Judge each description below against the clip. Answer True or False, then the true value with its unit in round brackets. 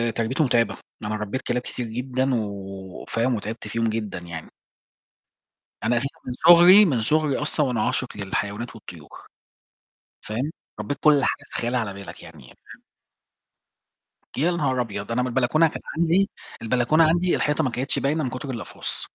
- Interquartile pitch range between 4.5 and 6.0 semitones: True (5.2 semitones)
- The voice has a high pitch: False (125 Hz)